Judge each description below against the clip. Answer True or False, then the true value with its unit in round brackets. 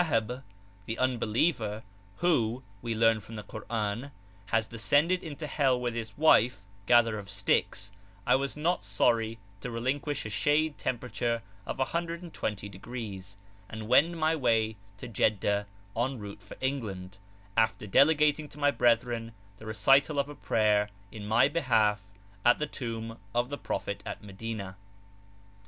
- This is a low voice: True (115 Hz)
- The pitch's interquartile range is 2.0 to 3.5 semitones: False (4.5 semitones)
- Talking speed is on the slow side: False (145 wpm)